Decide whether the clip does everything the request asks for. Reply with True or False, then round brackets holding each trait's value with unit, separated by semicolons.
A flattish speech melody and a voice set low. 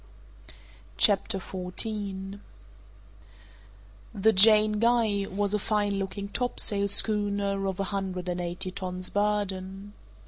False (1.5 semitones; 200 Hz)